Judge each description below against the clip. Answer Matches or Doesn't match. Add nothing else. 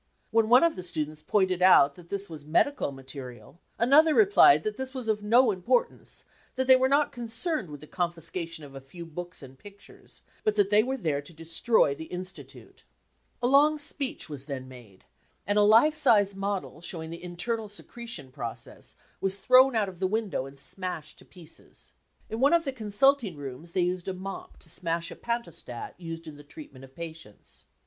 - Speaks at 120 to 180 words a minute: Doesn't match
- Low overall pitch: Doesn't match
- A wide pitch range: Matches